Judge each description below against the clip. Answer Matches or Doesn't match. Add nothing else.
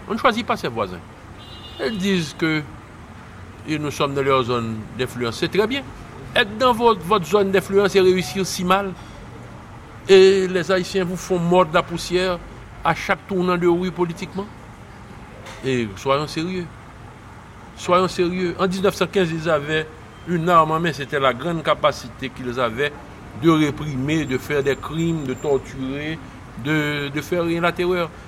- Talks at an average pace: Matches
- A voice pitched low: Doesn't match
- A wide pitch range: Matches